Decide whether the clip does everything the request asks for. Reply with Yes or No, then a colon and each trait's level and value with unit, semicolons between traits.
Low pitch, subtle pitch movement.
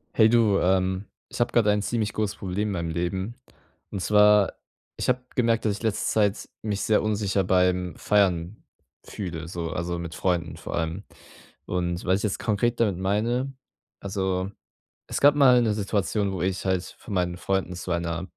No: low, 100 Hz; average, 3.0 semitones